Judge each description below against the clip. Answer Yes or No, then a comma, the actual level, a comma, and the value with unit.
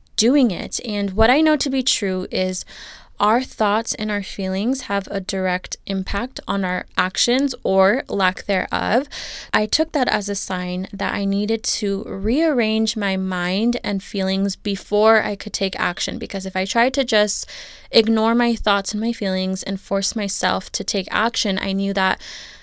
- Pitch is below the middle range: No, high, 205 Hz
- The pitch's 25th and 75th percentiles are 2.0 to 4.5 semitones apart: Yes, average, 2.9 semitones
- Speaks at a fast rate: No, average, 175 wpm